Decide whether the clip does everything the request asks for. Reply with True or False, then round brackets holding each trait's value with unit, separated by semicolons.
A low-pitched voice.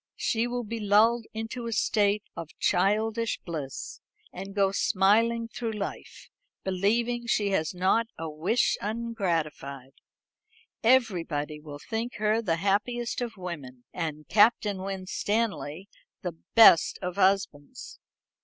False (200 Hz)